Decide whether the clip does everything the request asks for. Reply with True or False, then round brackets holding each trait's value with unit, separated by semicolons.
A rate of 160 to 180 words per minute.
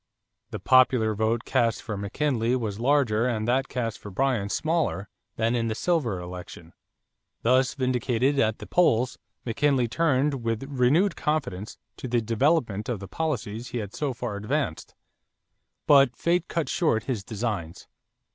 False (150 wpm)